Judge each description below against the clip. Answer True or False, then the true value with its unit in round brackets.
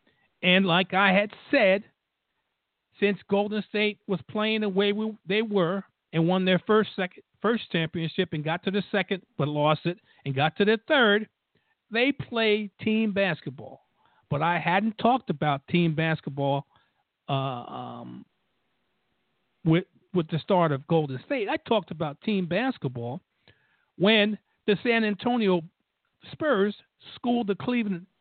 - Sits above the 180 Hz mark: True (190 Hz)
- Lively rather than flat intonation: False (4.5 semitones)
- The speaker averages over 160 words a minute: False (145 wpm)